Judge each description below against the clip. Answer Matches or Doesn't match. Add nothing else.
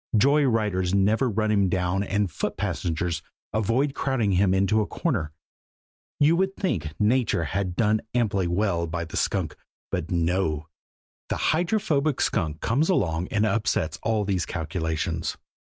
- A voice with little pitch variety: Doesn't match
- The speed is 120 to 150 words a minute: Matches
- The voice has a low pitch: Matches